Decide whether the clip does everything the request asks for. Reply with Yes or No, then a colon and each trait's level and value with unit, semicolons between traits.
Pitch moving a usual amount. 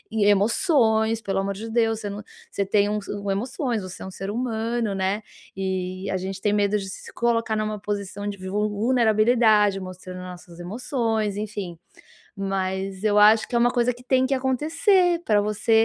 Yes: average, 3.0 semitones